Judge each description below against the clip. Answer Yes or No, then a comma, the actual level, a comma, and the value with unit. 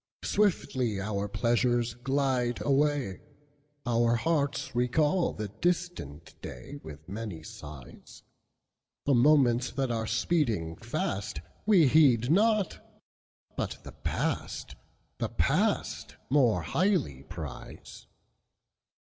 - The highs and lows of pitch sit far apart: Yes, wide, 5.7 semitones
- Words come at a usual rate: No, slow, 80 wpm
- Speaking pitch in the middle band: No, low, 125 Hz